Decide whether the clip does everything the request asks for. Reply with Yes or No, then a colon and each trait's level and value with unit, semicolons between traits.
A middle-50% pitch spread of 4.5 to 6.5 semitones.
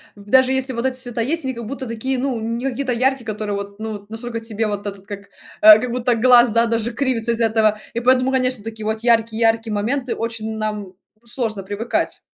No: narrow, 2.6 semitones